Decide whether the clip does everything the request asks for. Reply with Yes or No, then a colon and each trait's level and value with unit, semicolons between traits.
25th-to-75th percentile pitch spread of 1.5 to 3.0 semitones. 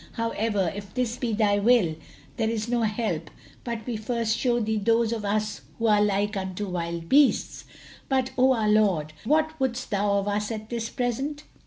Yes: average, 2.7 semitones